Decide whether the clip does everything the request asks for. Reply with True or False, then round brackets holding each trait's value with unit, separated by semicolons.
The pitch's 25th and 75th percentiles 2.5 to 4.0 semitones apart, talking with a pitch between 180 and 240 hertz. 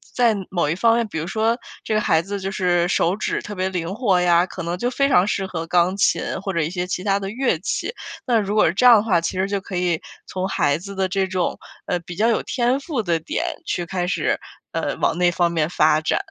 True (3.3 semitones; 185 Hz)